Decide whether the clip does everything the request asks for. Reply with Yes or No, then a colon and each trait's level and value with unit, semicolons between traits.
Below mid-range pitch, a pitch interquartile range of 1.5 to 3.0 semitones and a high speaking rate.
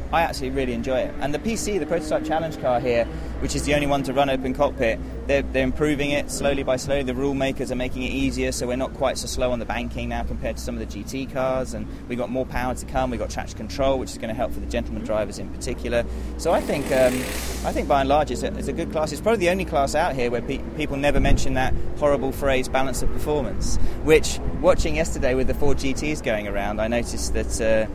Yes: low, 130 Hz; average, 2.7 semitones; fast, 260 wpm